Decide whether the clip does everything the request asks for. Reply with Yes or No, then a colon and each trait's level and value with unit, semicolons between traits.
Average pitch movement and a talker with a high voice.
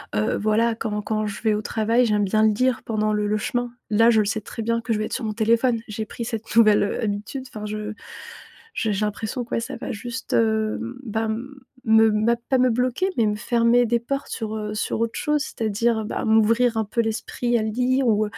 No: narrow, 1.8 semitones; high, 225 Hz